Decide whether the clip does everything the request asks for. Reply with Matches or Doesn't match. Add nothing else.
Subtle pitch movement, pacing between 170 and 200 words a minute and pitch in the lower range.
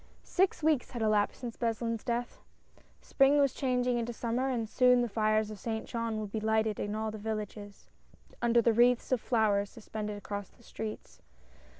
Doesn't match